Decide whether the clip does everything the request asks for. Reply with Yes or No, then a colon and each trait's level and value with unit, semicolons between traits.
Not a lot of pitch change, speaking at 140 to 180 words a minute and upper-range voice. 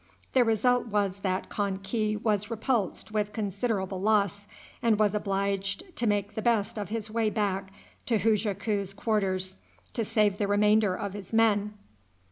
Yes: narrow, 1.7 semitones; average, 155 wpm; high, 210 Hz